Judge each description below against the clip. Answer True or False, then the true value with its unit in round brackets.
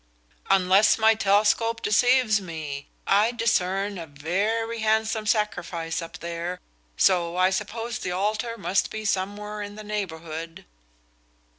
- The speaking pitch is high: True (205 Hz)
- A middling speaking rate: False (125 wpm)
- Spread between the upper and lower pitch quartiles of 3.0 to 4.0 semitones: True (3.5 semitones)